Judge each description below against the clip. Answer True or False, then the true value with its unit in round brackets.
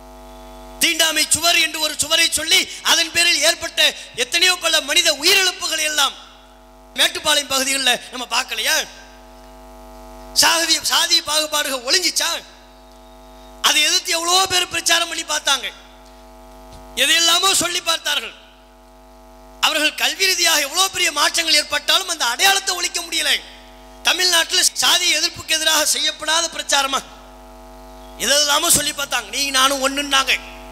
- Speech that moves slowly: True (100 wpm)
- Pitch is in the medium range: False (300 Hz)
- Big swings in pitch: True (8.7 semitones)